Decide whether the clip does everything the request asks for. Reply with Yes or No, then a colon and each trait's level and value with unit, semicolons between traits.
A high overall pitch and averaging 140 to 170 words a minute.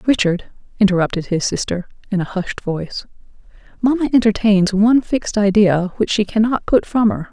Yes: high, 205 Hz; average, 155 wpm